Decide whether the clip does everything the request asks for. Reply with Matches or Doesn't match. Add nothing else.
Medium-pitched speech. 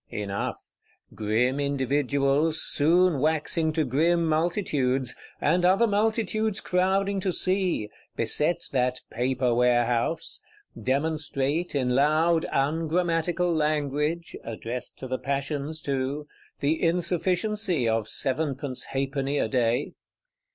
Matches